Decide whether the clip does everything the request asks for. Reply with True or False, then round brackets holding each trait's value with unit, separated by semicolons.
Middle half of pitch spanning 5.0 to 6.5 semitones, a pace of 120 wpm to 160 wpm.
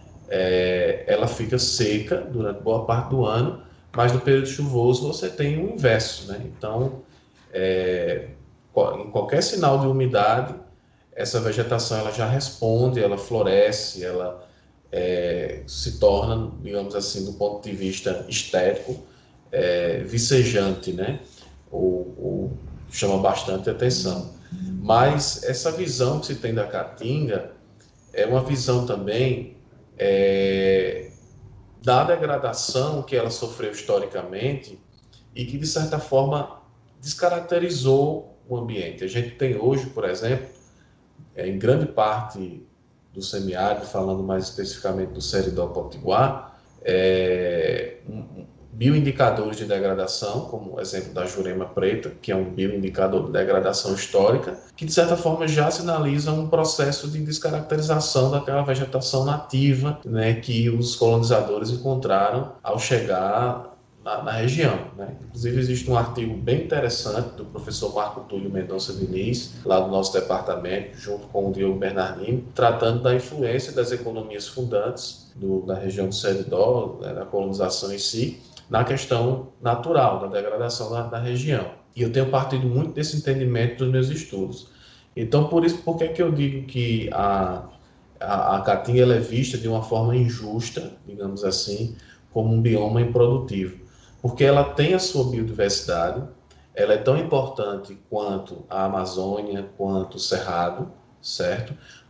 True (5.4 semitones; 140 wpm)